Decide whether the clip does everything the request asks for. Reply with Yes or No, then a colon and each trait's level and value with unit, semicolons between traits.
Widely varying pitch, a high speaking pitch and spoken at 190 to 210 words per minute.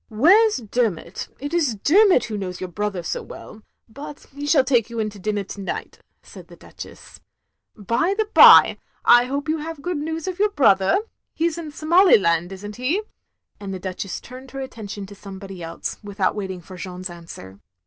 Yes: wide, 7.7 semitones; high, 220 Hz; average, 200 wpm